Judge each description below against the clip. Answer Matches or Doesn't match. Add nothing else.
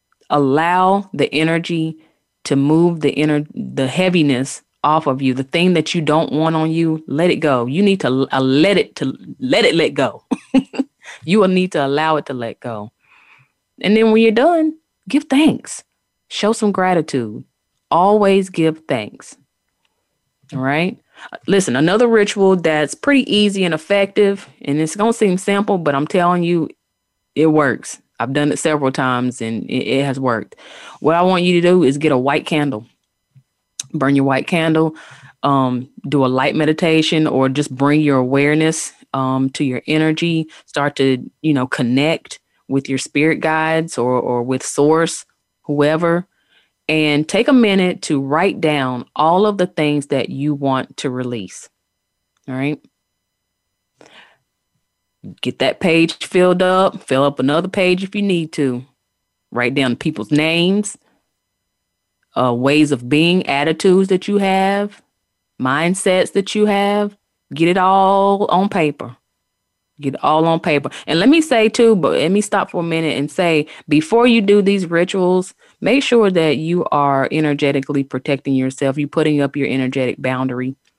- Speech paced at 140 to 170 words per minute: Matches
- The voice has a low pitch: Doesn't match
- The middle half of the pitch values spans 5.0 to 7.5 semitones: Matches